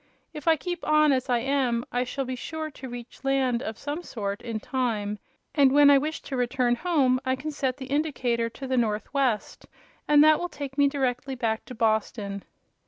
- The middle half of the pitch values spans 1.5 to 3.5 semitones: Yes, average, 3.1 semitones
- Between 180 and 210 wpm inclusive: Yes, average, 200 wpm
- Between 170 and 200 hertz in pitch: No, very high, 260 Hz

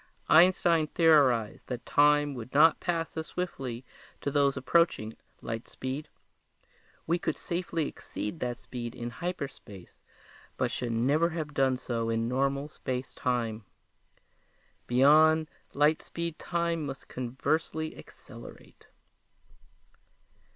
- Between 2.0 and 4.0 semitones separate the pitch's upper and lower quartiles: No, average, 4.5 semitones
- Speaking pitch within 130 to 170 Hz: Yes, medium, 140 Hz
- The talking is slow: Yes, slow, 115 wpm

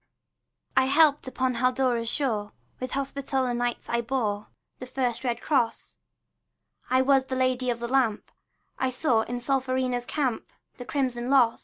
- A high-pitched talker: Yes, very high, 255 Hz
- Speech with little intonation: Yes, narrow, 1.9 semitones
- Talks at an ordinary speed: Yes, average, 150 wpm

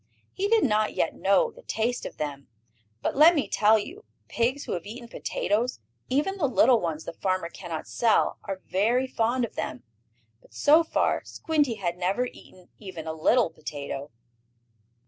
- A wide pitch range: Yes, wide, 6.6 semitones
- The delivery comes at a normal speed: Yes, average, 170 wpm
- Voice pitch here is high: Yes, high, 225 Hz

